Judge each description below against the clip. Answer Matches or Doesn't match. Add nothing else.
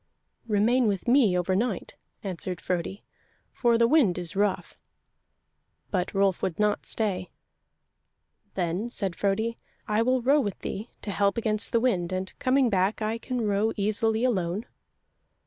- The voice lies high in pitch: Matches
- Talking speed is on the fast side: Doesn't match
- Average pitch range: Matches